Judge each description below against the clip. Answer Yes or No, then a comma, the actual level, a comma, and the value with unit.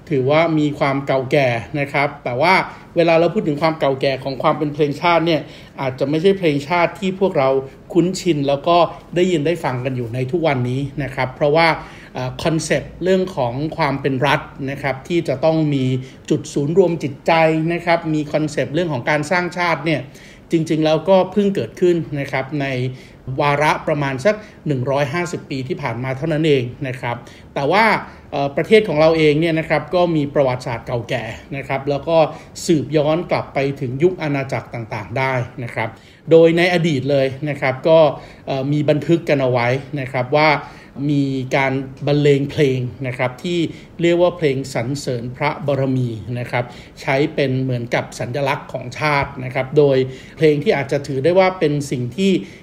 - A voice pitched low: No, medium, 145 Hz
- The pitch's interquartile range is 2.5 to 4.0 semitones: Yes, average, 3.4 semitones